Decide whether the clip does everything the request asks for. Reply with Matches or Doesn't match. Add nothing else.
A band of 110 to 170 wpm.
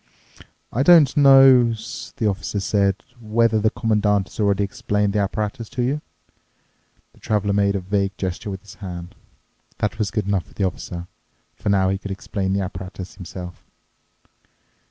Matches